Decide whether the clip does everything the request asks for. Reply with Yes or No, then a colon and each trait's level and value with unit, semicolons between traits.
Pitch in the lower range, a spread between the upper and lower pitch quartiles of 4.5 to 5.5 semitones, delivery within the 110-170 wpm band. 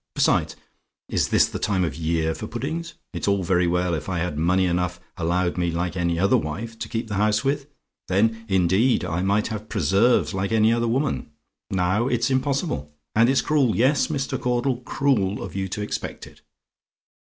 No: low, 100 Hz; average, 5.2 semitones; average, 190 wpm